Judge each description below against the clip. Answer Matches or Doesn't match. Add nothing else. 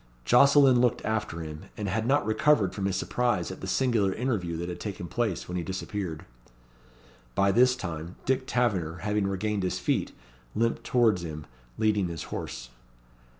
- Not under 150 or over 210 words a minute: Matches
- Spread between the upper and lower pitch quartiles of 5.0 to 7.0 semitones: Matches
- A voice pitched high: Doesn't match